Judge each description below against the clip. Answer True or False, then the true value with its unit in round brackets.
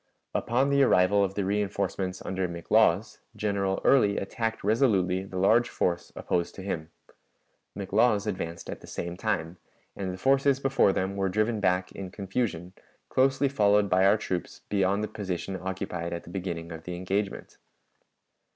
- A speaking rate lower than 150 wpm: False (160 wpm)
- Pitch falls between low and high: False (95 Hz)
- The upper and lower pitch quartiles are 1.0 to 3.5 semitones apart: True (2.7 semitones)